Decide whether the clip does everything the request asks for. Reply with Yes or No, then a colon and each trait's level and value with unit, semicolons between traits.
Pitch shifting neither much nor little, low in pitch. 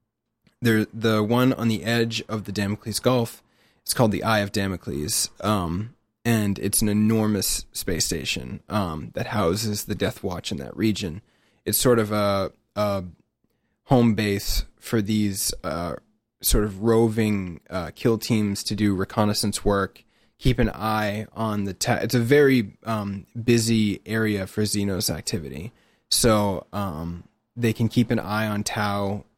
No: narrow, 2.2 semitones; low, 105 Hz